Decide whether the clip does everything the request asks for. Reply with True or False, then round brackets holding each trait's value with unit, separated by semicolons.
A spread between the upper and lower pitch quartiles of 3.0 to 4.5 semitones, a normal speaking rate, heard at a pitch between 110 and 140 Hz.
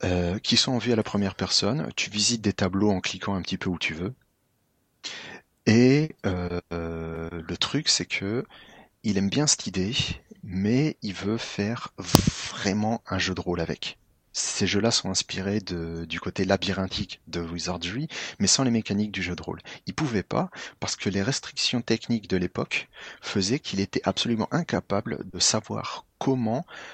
False (4.2 semitones; 175 wpm; 100 Hz)